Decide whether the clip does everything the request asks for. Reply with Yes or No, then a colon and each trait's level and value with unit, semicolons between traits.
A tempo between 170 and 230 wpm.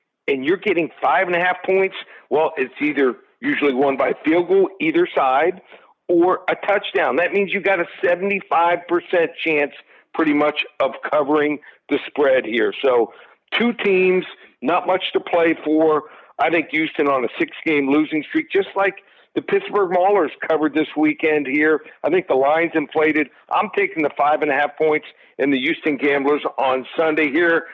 Yes: average, 175 wpm